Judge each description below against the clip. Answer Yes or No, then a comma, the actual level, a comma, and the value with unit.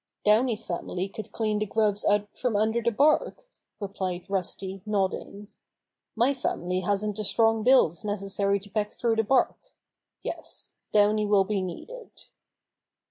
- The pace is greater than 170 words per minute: No, average, 140 wpm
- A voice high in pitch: Yes, high, 210 Hz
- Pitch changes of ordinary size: No, narrow, 2.2 semitones